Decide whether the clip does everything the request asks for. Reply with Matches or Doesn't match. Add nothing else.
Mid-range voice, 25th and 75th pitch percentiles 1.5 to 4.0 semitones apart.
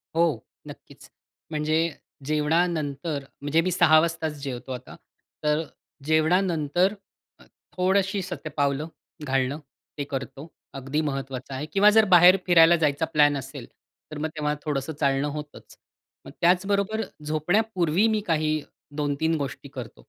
Matches